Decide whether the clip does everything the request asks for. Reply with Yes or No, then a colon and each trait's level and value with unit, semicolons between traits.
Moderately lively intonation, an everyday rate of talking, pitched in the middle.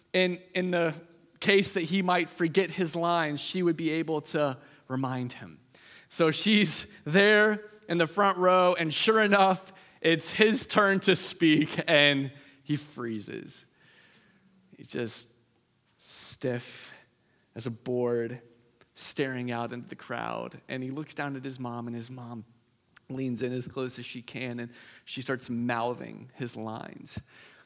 No: wide, 6.8 semitones; average, 150 wpm; medium, 145 Hz